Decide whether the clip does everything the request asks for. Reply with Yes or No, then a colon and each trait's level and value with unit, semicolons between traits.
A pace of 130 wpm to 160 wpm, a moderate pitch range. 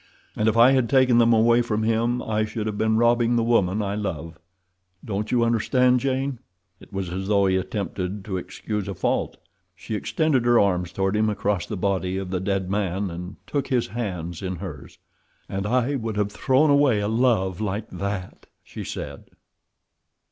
No: average, 185 wpm; average, 3.8 semitones